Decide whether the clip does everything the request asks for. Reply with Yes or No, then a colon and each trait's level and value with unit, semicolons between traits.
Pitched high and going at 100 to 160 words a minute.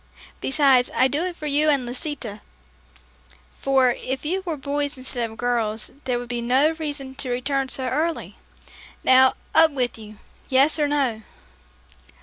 Yes: very high, 265 Hz; average, 155 wpm